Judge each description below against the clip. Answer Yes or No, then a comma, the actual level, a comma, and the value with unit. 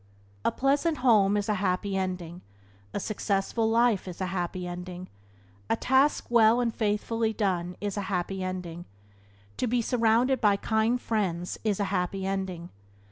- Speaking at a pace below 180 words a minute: Yes, average, 155 wpm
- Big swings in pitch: No, average, 3.7 semitones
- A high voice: Yes, high, 200 Hz